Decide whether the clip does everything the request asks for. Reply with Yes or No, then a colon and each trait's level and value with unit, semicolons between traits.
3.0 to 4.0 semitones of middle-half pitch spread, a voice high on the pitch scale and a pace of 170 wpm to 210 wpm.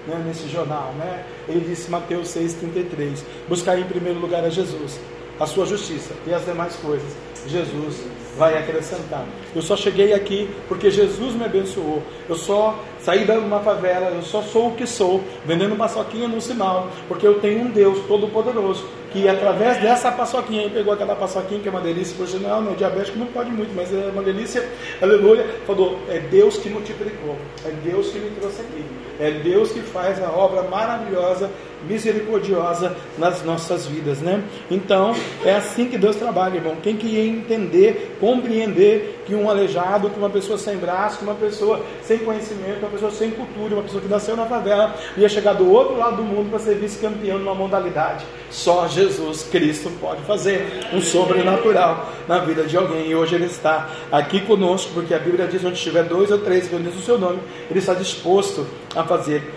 Yes: average, 3.7 semitones; high, 195 Hz; fast, 185 wpm